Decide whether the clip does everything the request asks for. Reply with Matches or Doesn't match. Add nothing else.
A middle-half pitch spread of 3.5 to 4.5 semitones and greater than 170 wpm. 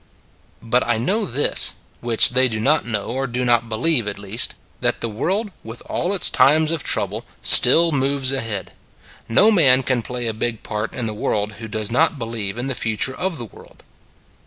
Matches